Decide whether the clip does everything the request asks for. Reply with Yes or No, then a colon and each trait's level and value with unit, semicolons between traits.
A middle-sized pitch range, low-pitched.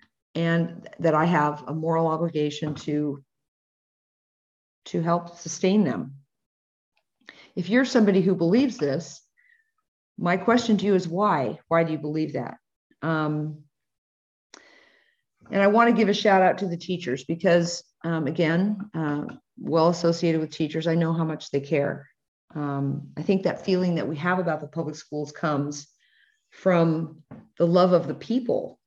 No: average, 3.6 semitones; medium, 165 Hz